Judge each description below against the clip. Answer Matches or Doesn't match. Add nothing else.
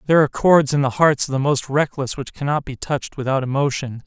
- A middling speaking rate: Doesn't match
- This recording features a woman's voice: Doesn't match